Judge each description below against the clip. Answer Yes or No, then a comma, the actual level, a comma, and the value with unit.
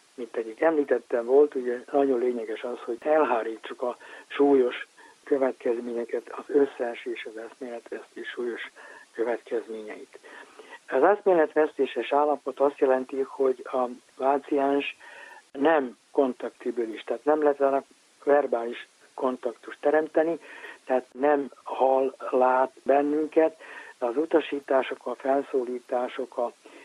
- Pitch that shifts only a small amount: No, average, 3.6 semitones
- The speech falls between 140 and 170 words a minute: No, average, 110 wpm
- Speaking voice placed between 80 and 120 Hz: No, medium, 140 Hz